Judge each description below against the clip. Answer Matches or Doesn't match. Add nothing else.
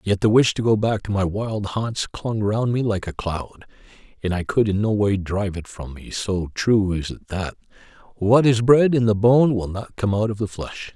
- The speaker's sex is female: Doesn't match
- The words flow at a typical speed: Doesn't match